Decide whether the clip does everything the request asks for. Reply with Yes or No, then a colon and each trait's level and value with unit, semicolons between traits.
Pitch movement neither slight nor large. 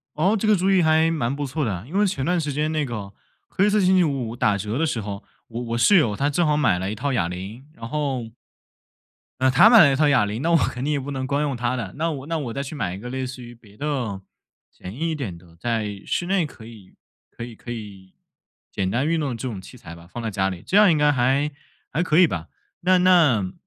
No: wide, 6.1 semitones